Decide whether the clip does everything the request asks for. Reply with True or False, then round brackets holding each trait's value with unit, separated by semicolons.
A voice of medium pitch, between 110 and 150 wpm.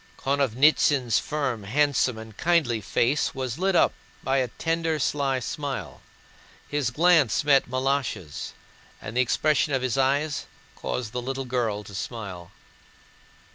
False (130 Hz; 135 wpm)